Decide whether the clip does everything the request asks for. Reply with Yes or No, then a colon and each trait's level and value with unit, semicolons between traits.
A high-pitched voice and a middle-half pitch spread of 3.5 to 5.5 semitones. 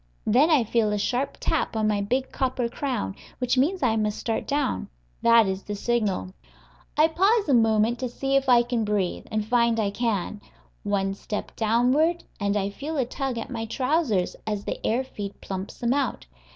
Yes: high, 235 Hz; average, 4.1 semitones